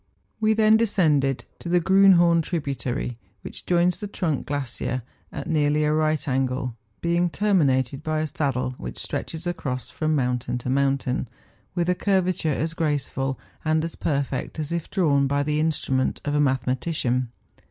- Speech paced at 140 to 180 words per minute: Yes, average, 160 wpm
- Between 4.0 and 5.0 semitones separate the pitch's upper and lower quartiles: Yes, average, 4.3 semitones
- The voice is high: No, medium, 150 Hz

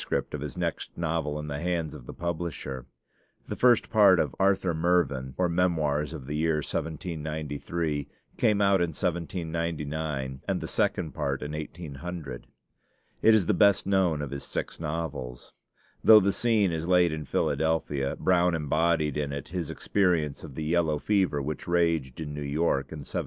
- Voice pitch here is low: Yes, very low, 80 Hz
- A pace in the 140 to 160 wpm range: No, average, 170 wpm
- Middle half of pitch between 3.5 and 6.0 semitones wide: No, average, 3.1 semitones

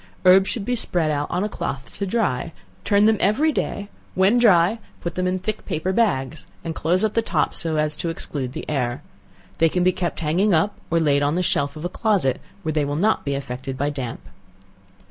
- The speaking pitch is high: No, medium, 170 Hz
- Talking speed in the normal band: No, fast, 220 wpm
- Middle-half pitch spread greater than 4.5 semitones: Yes, wide, 5.4 semitones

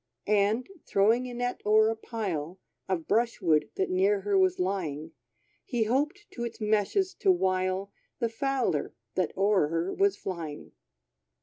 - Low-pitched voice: No, high, 205 Hz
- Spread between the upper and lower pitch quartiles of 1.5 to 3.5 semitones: No, average, 4.2 semitones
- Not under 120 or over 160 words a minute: Yes, average, 150 wpm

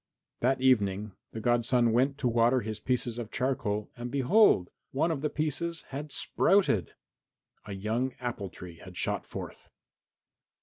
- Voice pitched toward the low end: Yes, low, 120 Hz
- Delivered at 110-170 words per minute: Yes, average, 145 wpm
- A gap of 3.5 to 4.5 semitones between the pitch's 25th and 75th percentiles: Yes, average, 4.0 semitones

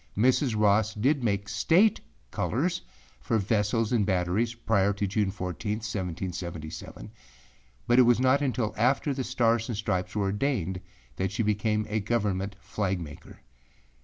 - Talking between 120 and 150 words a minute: Yes, average, 145 wpm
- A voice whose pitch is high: No, low, 105 Hz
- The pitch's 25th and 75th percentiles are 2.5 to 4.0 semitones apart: Yes, average, 3.4 semitones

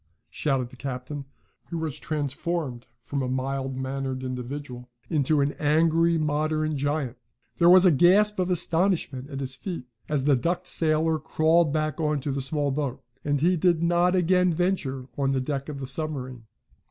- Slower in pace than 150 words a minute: No, average, 165 wpm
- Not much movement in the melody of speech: No, average, 3.7 semitones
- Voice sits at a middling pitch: Yes, medium, 150 Hz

